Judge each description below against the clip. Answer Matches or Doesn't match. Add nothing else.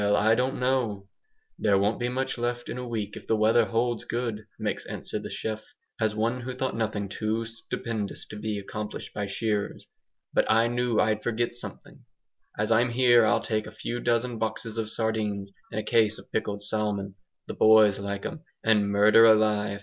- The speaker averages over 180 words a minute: Matches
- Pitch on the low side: Matches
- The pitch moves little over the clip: Matches